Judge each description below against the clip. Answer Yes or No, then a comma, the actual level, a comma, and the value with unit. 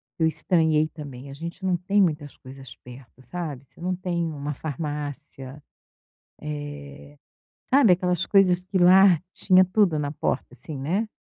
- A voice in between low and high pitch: Yes, medium, 155 Hz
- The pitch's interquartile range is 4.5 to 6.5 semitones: No, average, 4.0 semitones